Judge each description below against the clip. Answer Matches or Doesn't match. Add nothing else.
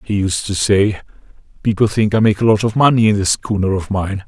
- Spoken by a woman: Doesn't match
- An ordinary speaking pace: Doesn't match